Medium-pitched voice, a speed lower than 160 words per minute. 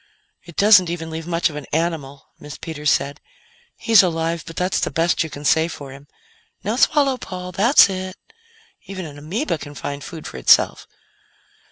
No: medium, 165 Hz; average, 180 wpm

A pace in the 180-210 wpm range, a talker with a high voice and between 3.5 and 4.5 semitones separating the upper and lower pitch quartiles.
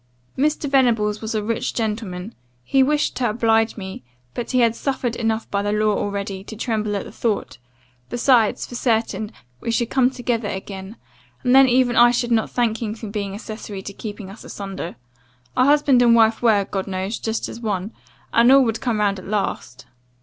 No: average, 195 wpm; high, 225 Hz; average, 2.8 semitones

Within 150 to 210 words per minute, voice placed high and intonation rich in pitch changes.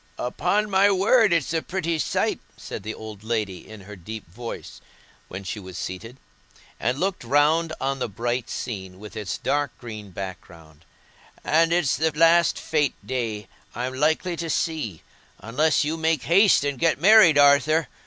No: average, 165 wpm; low, 135 Hz; wide, 7.1 semitones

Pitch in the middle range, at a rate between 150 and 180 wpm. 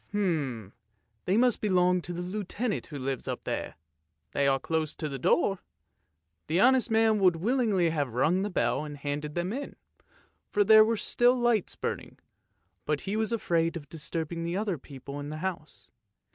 Yes: medium, 175 Hz; average, 175 wpm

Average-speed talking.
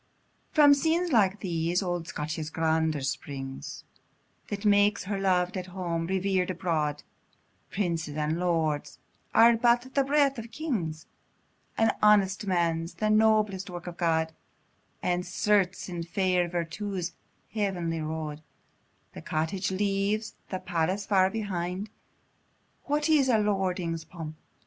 No: slow, 125 wpm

